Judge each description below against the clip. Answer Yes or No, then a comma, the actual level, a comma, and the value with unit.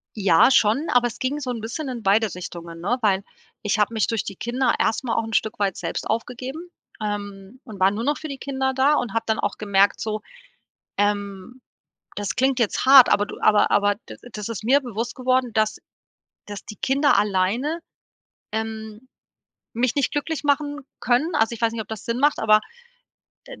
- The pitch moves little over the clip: No, average, 4.0 semitones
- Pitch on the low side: No, high, 225 Hz